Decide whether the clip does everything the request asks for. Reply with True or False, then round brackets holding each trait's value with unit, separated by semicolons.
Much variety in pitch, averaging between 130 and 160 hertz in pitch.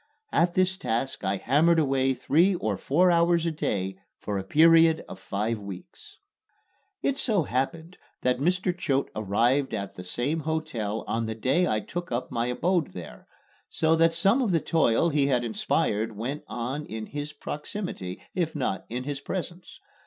True (6.8 semitones; 140 Hz)